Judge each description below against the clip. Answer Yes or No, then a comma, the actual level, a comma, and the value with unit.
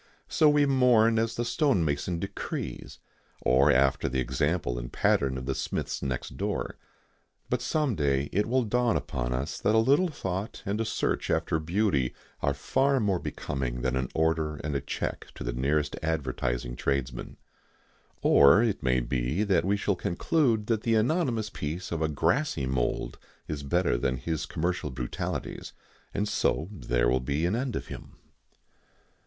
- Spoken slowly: No, average, 165 wpm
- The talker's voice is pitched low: Yes, very low, 80 Hz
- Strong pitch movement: Yes, wide, 8.9 semitones